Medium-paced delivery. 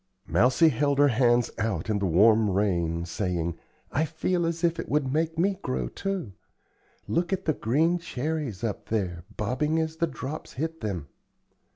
Yes: average, 170 wpm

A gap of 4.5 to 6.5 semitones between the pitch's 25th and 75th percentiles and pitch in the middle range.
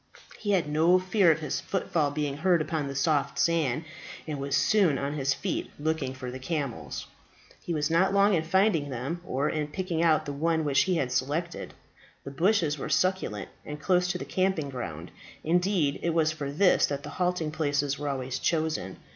No: average, 3.7 semitones; medium, 155 Hz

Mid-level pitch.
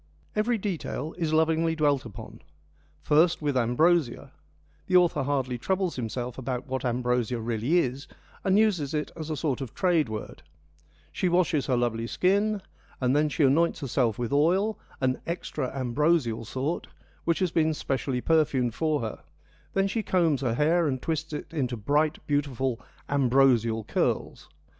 Yes: medium, 145 Hz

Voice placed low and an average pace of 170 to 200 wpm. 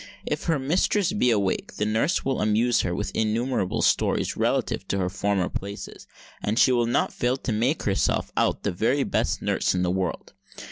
Yes: low, 110 Hz; average, 190 wpm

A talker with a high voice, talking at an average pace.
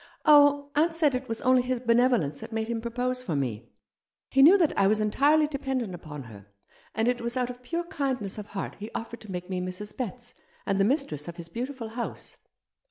No: high, 235 Hz; fast, 215 wpm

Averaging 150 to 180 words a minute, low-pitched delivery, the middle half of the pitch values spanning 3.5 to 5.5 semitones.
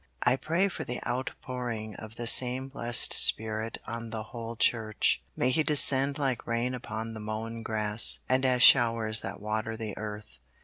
No: average, 170 wpm; low, 115 Hz; narrow, 2.6 semitones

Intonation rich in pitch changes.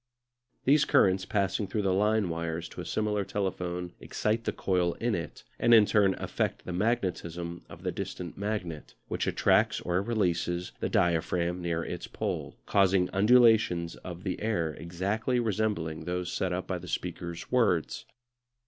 No: average, 3.5 semitones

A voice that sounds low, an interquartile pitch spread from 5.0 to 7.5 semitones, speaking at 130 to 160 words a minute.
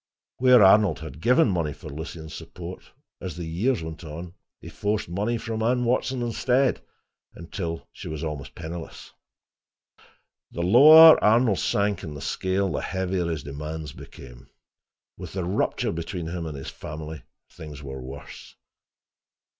Yes: very low, 85 Hz; wide, 5.4 semitones; average, 145 wpm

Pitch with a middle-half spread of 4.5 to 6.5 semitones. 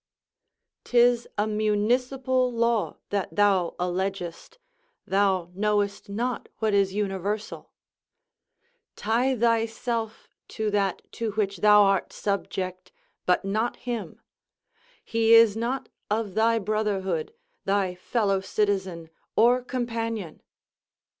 No: average, 2.8 semitones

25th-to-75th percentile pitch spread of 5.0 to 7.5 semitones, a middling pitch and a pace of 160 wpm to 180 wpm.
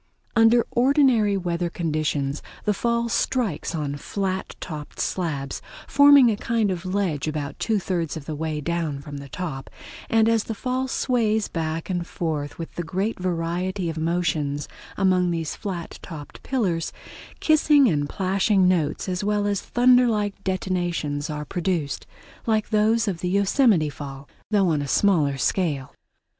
No: average, 5.3 semitones; medium, 180 Hz; average, 150 wpm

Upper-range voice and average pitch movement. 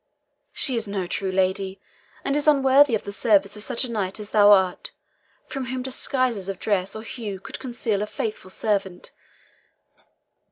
Yes: high, 210 Hz; average, 4.4 semitones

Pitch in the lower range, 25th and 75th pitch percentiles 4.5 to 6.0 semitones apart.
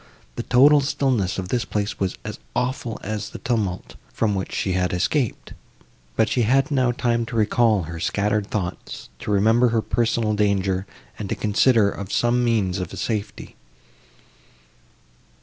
No: low, 110 Hz; average, 3.5 semitones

